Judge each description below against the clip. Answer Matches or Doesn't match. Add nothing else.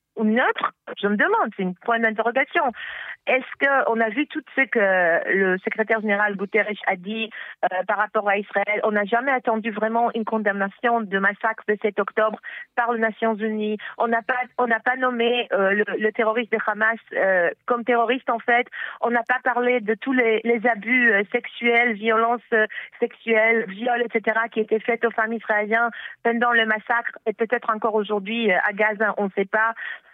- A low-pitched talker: Doesn't match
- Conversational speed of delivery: Doesn't match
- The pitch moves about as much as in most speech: Doesn't match